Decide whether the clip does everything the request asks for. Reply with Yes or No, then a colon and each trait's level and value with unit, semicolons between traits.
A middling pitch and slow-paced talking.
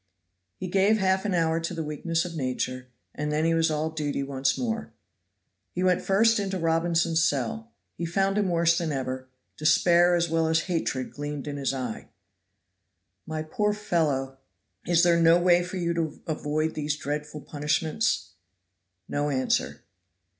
No: medium, 165 Hz; average, 160 wpm